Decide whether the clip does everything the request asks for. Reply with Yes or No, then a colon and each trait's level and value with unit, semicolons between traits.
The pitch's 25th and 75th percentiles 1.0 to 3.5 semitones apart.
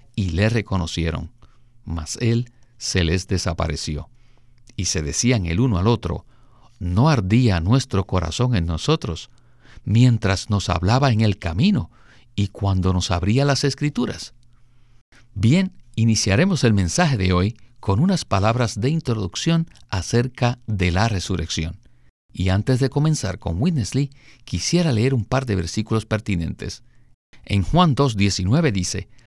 No: average, 4.9 semitones